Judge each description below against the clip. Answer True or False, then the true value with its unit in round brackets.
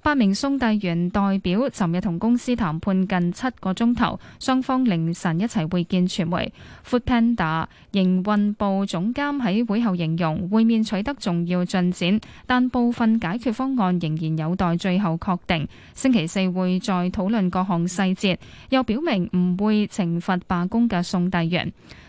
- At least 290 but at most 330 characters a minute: False (260 characters per minute)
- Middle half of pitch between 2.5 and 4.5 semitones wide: True (4.2 semitones)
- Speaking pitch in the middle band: False (195 Hz)